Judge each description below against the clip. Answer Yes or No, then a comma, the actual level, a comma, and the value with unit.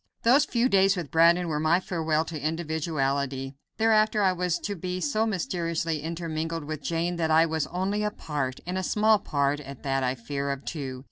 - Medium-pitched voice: Yes, medium, 165 Hz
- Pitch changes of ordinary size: Yes, average, 3.9 semitones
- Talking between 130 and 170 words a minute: No, average, 195 wpm